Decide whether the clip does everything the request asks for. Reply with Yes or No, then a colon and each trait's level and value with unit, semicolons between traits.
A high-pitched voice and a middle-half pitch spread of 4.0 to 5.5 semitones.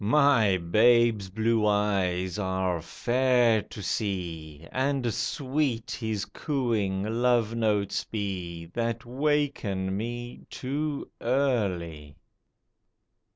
No: low, 110 Hz; average, 4.4 semitones